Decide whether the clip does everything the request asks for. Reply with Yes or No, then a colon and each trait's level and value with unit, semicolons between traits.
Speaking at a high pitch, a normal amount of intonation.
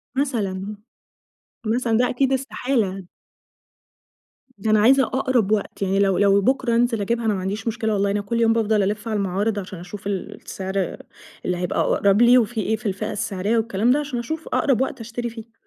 Yes: high, 220 Hz; average, 3.2 semitones